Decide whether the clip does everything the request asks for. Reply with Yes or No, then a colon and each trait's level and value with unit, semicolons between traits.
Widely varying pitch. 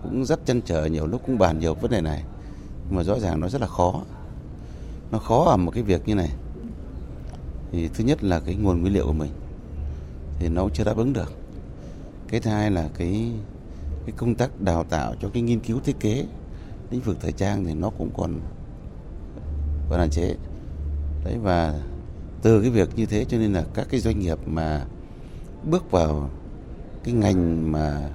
Yes: wide, 5.9 semitones